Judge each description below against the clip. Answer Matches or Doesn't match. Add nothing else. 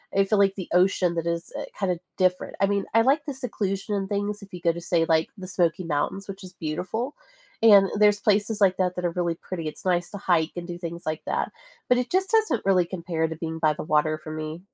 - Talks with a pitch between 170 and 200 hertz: Matches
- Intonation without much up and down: Doesn't match